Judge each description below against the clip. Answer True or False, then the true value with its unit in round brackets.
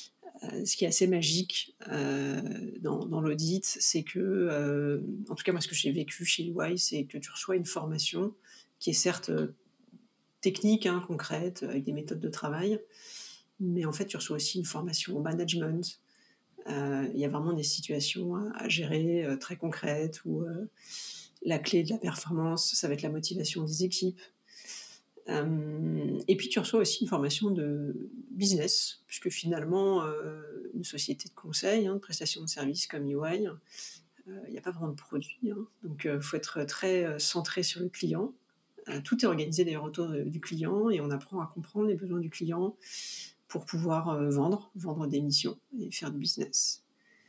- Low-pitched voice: False (170 Hz)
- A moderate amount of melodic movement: True (4.1 semitones)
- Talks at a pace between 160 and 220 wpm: True (175 wpm)